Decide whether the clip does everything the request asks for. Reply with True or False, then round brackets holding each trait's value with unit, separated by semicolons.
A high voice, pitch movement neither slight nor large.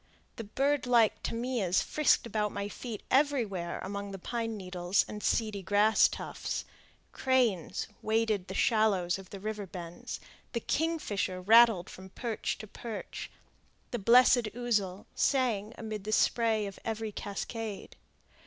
True (215 Hz; 3.1 semitones)